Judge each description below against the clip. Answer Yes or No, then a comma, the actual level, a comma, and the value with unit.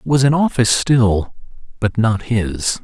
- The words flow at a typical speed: Yes, average, 170 wpm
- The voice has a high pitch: No, low, 115 Hz